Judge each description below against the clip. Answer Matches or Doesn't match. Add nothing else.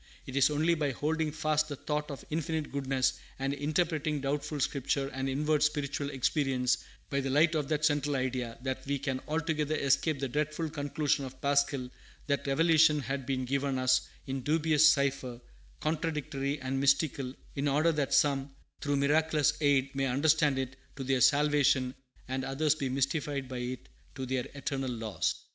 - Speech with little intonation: Matches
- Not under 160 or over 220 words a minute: Matches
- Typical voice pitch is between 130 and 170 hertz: Matches